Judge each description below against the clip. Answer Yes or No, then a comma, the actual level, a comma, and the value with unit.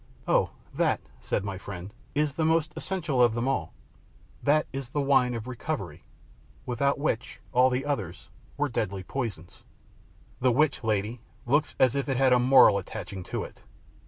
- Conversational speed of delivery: Yes, average, 165 wpm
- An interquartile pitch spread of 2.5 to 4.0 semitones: No, average, 4.5 semitones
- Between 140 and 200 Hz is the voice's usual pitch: No, low, 125 Hz